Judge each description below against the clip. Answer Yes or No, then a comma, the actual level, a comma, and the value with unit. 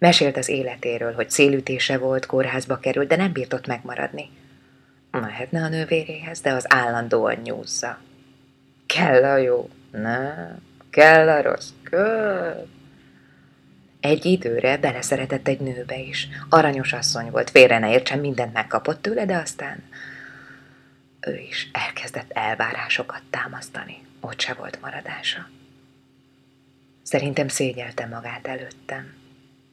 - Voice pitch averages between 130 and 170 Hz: Yes, low, 135 Hz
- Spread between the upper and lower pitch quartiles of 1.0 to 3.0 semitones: Yes, narrow, 2.4 semitones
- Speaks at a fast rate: No, average, 115 wpm